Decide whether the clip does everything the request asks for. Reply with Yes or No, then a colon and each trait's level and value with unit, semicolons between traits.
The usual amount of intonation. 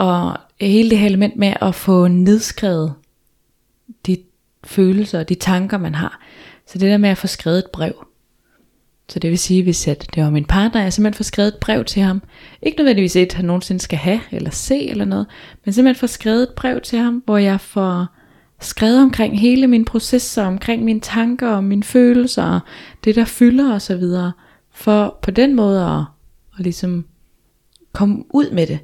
Yes: average, 3.9 semitones